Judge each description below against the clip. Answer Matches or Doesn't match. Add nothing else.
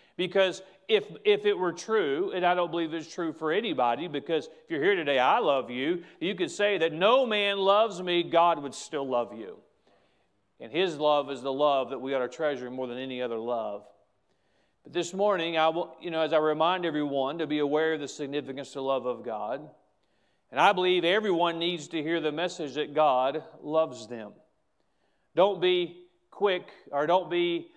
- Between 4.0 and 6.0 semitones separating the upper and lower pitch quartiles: Matches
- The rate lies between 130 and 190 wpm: Doesn't match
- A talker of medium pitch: Matches